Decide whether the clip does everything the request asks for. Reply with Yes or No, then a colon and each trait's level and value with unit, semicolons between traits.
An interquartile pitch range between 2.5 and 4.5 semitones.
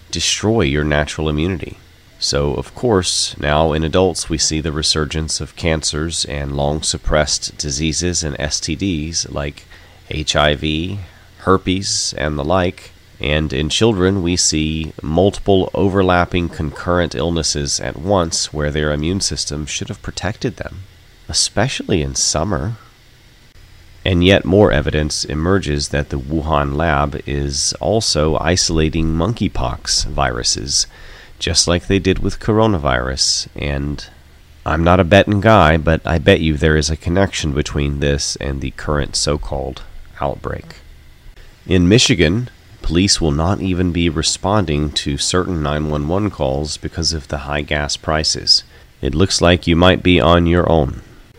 Yes: average, 4.0 semitones